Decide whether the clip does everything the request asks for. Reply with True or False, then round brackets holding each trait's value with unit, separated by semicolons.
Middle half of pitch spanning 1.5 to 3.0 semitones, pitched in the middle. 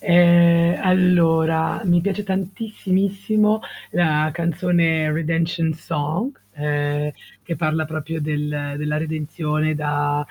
True (2.7 semitones; 165 Hz)